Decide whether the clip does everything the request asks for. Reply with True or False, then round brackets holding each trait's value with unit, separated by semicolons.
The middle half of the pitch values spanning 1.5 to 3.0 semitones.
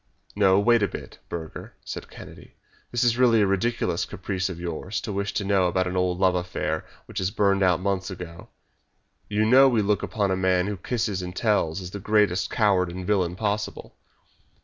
True (2.5 semitones)